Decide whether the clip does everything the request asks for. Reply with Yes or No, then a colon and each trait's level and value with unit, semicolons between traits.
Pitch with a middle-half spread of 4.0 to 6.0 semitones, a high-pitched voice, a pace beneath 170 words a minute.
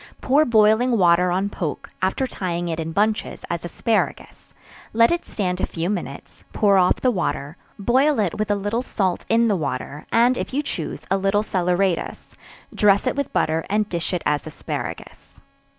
No: average, 4.6 semitones; high, 195 Hz; average, 180 wpm